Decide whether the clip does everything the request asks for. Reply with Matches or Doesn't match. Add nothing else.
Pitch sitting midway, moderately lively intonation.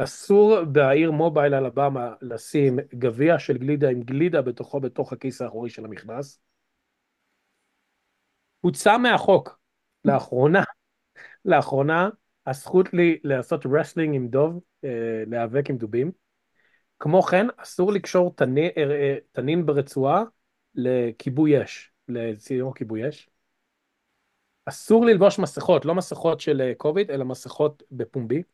Matches